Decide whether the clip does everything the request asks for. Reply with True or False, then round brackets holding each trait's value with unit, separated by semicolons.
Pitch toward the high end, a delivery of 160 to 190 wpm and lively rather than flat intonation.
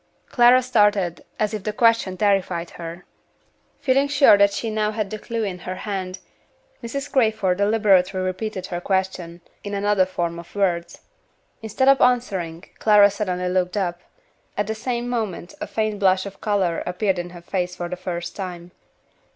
False (195 Hz; 165 wpm; 3.2 semitones)